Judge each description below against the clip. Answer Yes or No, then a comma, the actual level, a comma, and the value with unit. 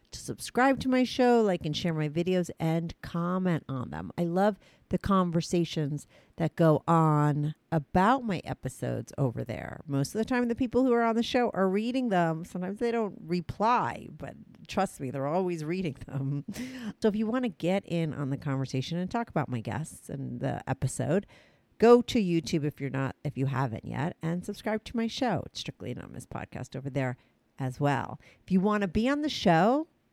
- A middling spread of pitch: No, wide, 7.2 semitones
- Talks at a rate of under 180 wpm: No, average, 200 wpm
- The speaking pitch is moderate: Yes, medium, 170 Hz